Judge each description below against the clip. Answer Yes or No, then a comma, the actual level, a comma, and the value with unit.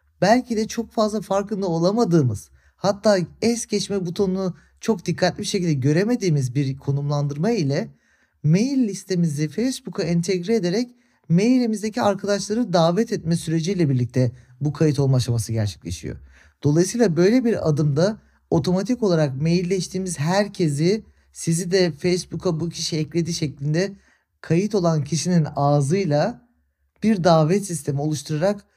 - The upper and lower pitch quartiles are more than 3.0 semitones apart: Yes, average, 5.3 semitones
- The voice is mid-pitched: Yes, medium, 175 Hz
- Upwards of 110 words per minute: Yes, average, 120 wpm